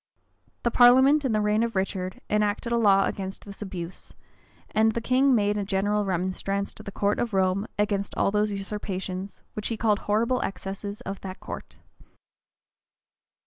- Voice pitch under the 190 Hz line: No, high, 205 Hz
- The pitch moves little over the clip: Yes, narrow, 2.3 semitones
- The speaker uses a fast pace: No, average, 165 wpm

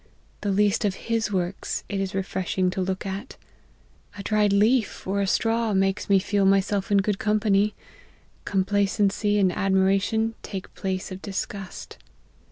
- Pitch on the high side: Yes, high, 200 Hz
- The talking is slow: No, average, 155 wpm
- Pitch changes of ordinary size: No, narrow, 1.5 semitones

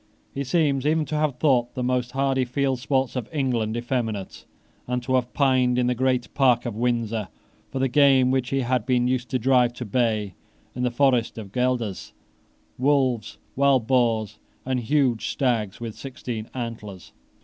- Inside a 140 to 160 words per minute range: No, average, 175 wpm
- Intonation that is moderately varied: No, narrow, 2.1 semitones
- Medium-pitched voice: No, low, 125 Hz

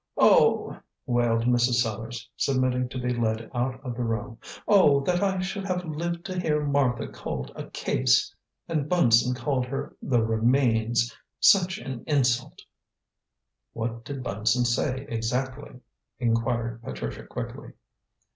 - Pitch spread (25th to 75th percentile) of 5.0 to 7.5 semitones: No, average, 3.5 semitones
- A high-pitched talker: No, low, 125 Hz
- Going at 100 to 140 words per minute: Yes, slow, 135 wpm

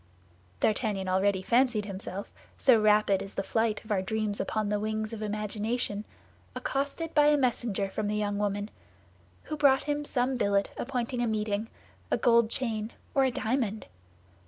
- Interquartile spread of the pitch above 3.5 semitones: No, average, 3.1 semitones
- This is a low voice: No, high, 215 Hz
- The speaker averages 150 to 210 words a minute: Yes, average, 160 wpm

